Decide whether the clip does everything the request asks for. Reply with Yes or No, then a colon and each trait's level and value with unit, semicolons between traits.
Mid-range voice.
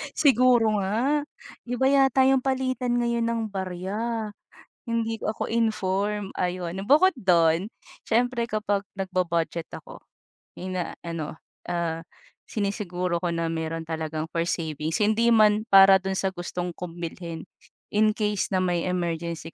No: high, 195 Hz